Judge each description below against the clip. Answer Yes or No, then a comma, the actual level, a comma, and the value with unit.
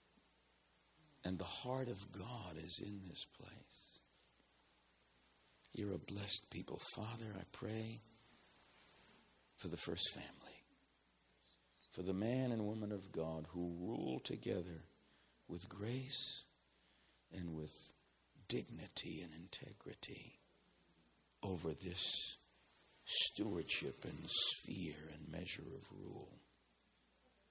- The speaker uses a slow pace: Yes, slow, 100 wpm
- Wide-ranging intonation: Yes, wide, 6.3 semitones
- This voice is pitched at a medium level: No, very low, 90 Hz